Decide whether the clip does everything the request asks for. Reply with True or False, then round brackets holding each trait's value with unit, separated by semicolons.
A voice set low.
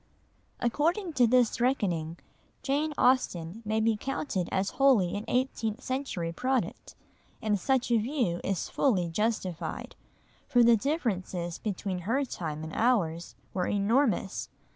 False (220 Hz)